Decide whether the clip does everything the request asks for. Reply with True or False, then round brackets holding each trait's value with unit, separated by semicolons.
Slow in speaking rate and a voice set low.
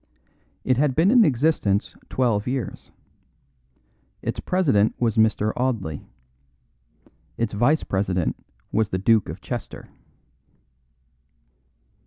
True (100 wpm; 115 Hz)